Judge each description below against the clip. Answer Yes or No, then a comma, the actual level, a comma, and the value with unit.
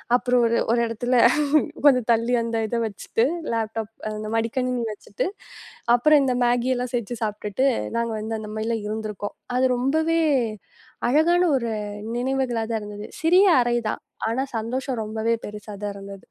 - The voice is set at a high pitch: Yes, high, 230 Hz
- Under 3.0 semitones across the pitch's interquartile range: Yes, narrow, 2.6 semitones